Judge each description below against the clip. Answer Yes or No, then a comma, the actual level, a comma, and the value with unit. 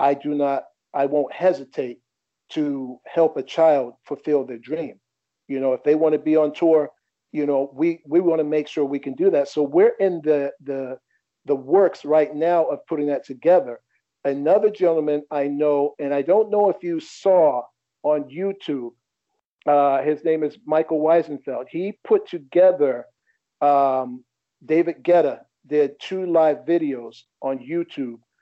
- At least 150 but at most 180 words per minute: Yes, average, 165 wpm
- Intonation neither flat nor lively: Yes, average, 3.2 semitones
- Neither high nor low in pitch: Yes, medium, 150 Hz